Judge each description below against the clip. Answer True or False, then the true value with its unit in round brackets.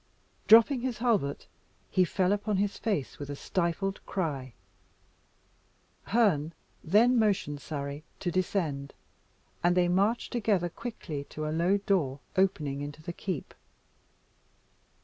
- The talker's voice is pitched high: False (180 Hz)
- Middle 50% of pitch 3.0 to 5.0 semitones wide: False (5.6 semitones)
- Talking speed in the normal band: False (125 wpm)